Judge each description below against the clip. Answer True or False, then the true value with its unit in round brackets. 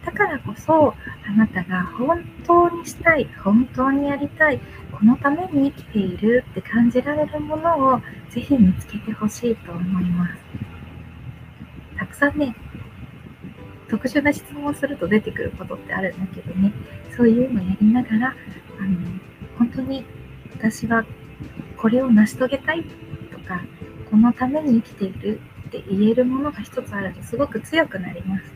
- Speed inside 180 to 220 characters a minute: False (310 characters per minute)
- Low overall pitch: False (235 Hz)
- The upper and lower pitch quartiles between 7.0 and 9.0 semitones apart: False (5.4 semitones)